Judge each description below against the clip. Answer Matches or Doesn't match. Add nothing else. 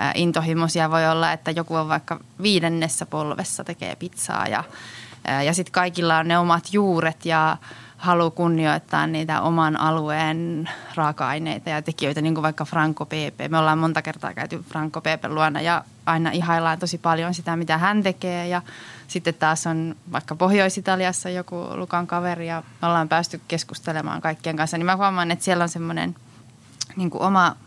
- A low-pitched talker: Doesn't match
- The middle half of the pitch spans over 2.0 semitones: Doesn't match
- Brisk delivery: Matches